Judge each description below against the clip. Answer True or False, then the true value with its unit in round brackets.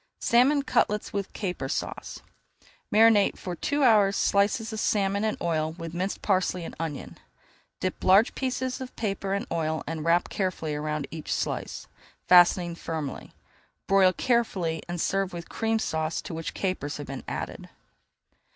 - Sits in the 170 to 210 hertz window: True (185 Hz)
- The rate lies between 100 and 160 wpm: True (155 wpm)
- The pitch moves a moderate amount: True (4.3 semitones)